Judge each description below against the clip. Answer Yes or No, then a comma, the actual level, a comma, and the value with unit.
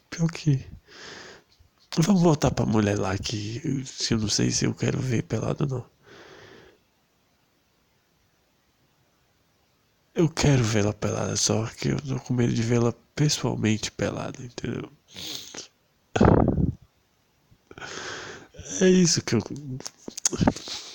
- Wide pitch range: Yes, wide, 5.8 semitones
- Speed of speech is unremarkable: No, slow, 110 wpm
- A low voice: Yes, low, 125 Hz